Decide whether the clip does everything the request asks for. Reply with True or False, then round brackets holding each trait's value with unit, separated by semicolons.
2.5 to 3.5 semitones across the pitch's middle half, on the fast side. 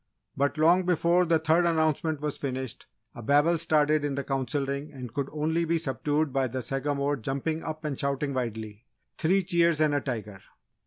False (2.9 semitones; 180 wpm)